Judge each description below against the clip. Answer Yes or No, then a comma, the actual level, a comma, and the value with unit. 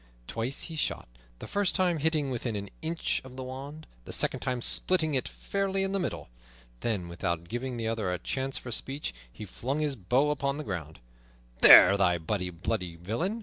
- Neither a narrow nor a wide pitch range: No, wide, 7.6 semitones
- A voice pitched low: Yes, low, 130 Hz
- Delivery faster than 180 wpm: Yes, average, 190 wpm